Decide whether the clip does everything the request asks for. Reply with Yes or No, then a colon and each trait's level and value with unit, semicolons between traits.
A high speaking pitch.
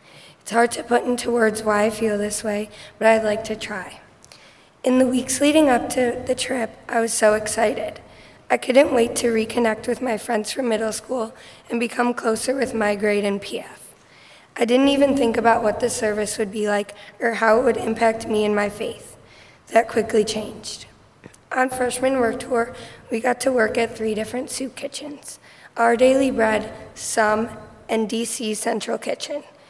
Yes: high, 230 Hz